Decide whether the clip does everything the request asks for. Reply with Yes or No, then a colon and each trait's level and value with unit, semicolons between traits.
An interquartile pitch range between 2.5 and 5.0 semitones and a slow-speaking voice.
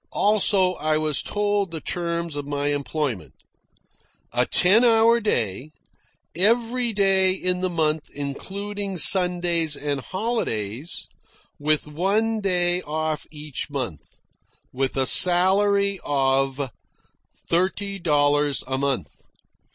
No: wide, 5.4 semitones; slow, 110 wpm